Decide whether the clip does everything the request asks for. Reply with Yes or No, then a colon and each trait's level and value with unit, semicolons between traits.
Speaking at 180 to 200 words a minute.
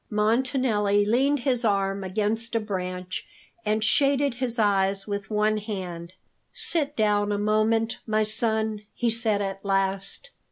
No: slow, 135 wpm